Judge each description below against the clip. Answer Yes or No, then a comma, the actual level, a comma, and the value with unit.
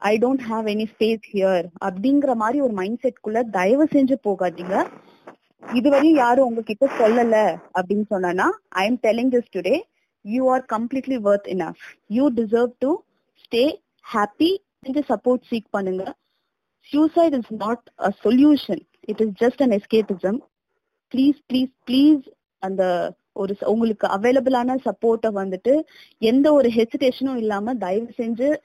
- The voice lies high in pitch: Yes, high, 235 Hz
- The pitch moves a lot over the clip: No, average, 4.5 semitones